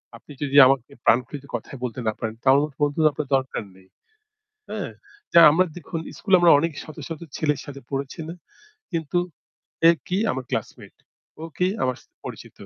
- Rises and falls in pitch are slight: No, average, 3.7 semitones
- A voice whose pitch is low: No, medium, 145 Hz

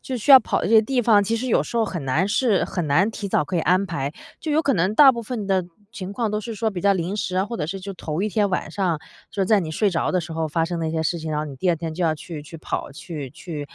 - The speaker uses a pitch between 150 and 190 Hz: Yes, medium, 185 Hz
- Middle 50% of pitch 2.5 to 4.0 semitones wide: No, average, 4.7 semitones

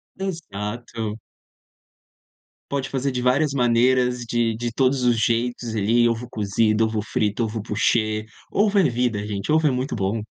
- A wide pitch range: No, average, 2.9 semitones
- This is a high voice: No, low, 120 Hz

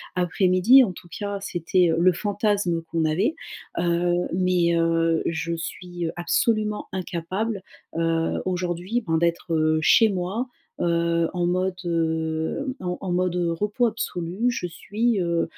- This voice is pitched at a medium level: Yes, medium, 175 Hz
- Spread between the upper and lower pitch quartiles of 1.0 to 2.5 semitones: No, average, 2.9 semitones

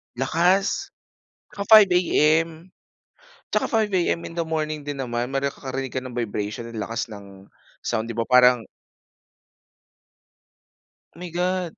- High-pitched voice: No, medium, 140 Hz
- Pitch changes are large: Yes, wide, 6.4 semitones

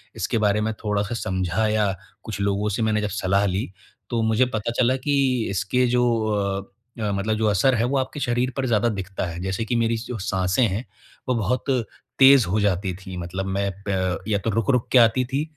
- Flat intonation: No, average, 3.6 semitones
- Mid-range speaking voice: No, low, 110 Hz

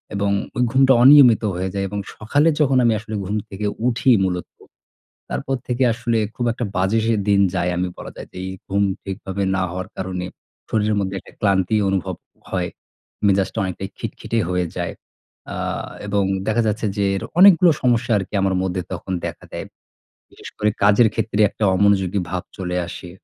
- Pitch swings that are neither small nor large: Yes, average, 3.5 semitones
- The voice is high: No, low, 100 Hz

